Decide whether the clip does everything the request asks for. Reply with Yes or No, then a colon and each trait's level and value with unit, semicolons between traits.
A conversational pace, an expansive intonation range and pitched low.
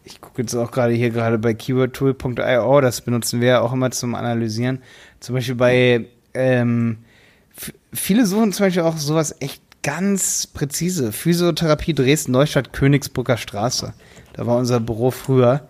No: average, 155 wpm; average, 3.0 semitones; low, 130 Hz